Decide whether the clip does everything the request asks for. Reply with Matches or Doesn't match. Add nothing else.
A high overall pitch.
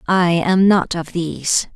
Doesn't match